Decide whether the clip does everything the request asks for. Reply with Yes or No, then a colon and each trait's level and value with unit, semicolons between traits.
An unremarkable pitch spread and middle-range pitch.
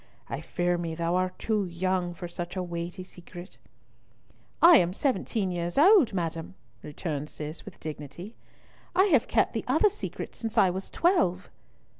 Yes: average, 3.6 semitones; medium, 180 Hz